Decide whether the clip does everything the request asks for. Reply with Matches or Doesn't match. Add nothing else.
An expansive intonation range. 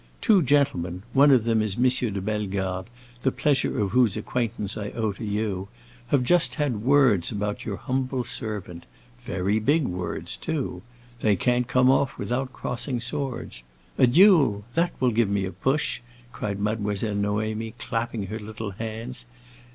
Doesn't match